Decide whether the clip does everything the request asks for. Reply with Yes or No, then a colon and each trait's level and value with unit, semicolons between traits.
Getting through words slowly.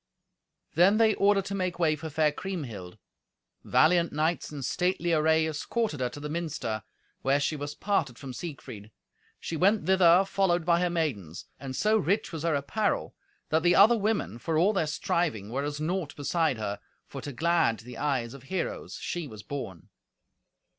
No: average, 175 wpm